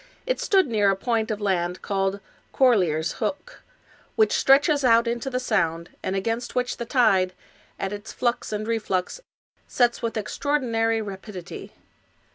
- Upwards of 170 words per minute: No, average, 150 wpm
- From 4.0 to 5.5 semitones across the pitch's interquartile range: Yes, average, 4.3 semitones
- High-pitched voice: Yes, high, 225 Hz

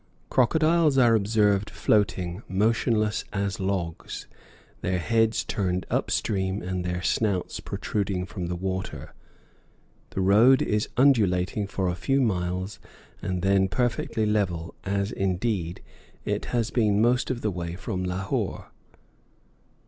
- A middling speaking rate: No, slow, 125 wpm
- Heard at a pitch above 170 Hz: No, low, 100 Hz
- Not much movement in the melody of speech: No, average, 3.4 semitones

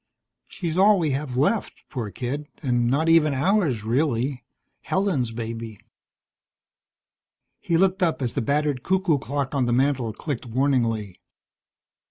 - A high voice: No, medium, 140 Hz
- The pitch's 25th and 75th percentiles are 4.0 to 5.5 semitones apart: Yes, average, 4.9 semitones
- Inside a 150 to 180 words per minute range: No, slow, 135 wpm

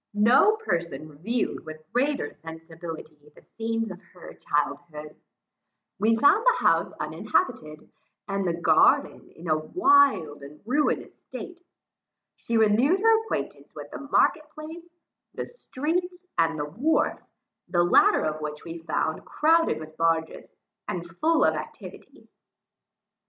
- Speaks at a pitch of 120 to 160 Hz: No, medium, 185 Hz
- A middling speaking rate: No, slow, 130 wpm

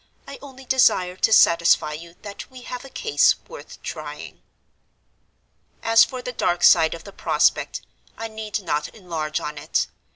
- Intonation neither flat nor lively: No, wide, 6.8 semitones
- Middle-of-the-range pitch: No, high, 200 Hz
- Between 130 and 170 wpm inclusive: Yes, average, 160 wpm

